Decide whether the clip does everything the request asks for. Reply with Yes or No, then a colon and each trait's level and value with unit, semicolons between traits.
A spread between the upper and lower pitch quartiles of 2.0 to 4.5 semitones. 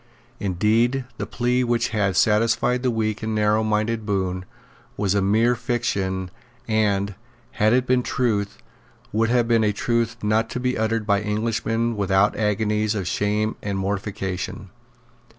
Yes: narrow, 2.4 semitones